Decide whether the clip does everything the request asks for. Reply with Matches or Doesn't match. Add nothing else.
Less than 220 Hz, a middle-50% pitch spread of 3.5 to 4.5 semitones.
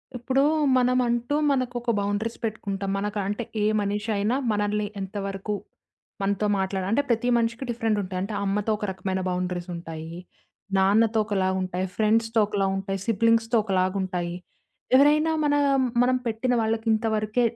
Doesn't match